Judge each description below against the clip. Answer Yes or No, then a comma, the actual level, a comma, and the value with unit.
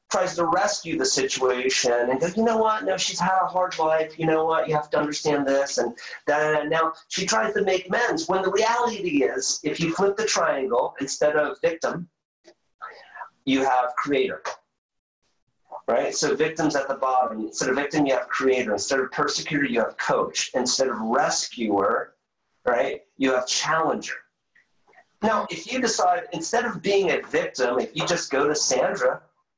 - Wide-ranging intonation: Yes, wide, 6.7 semitones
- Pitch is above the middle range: No, medium, 160 Hz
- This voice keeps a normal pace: Yes, average, 175 wpm